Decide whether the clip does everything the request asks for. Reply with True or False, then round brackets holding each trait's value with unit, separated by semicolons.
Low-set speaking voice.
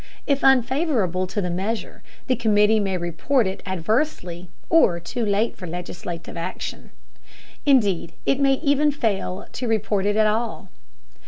False (210 Hz)